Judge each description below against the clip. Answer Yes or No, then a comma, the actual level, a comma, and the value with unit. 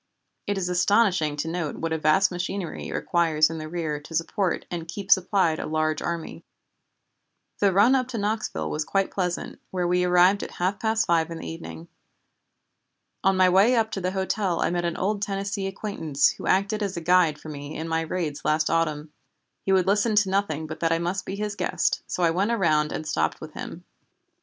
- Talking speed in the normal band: No, fast, 210 wpm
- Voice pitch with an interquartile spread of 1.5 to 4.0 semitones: Yes, average, 3.7 semitones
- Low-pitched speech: No, medium, 180 Hz